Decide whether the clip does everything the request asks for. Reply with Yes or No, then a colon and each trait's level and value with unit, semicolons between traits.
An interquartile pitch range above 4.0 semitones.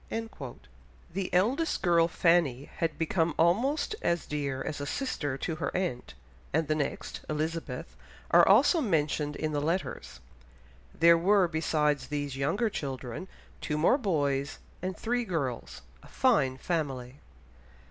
Yes: average, 4.5 semitones